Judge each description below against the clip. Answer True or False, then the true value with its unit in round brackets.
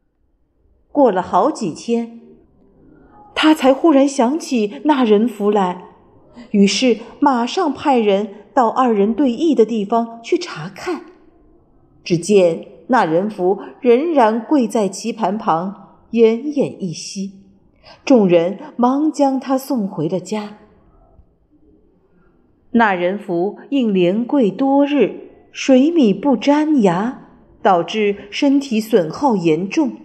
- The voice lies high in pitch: True (230 Hz)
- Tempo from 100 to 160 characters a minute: True (155 characters per minute)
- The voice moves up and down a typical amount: False (5.9 semitones)